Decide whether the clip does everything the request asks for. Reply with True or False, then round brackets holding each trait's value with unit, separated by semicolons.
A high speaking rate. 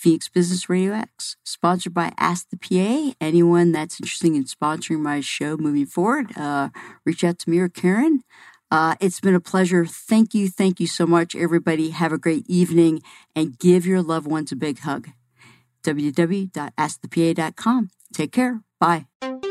False (165 wpm)